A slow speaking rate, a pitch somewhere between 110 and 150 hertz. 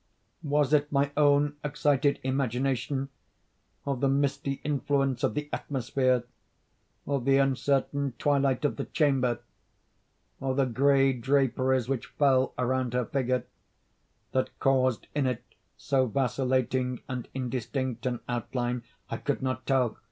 Yes: slow, 115 wpm; low, 135 Hz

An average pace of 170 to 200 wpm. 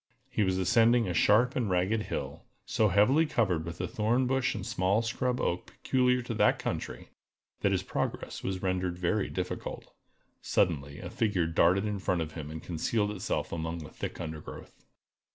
Yes: average, 175 wpm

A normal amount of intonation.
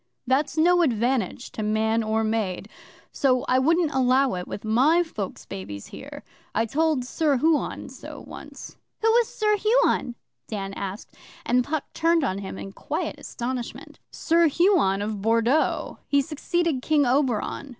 No: wide, 6.5 semitones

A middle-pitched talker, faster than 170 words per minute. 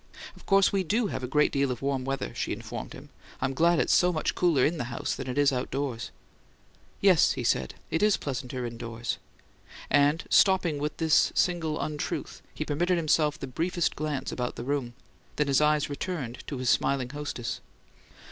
Yes: medium, 145 Hz; average, 185 wpm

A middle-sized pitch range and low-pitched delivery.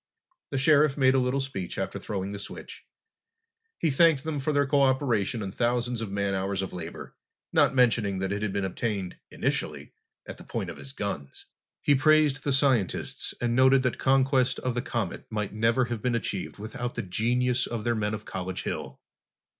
Yes: average, 4.7 semitones; low, 120 Hz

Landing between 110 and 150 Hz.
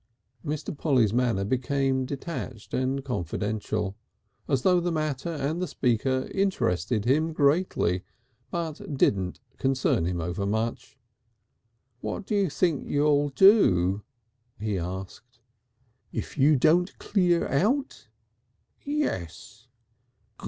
Yes: low, 135 Hz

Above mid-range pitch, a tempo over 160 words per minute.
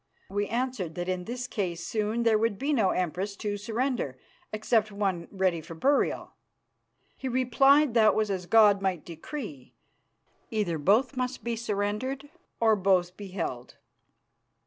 No: high, 210 Hz; average, 145 wpm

